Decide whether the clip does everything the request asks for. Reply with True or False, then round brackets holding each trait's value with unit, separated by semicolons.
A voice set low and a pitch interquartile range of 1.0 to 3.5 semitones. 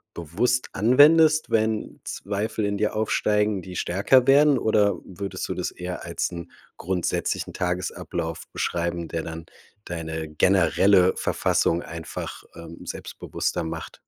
False (95 Hz; 4.3 semitones)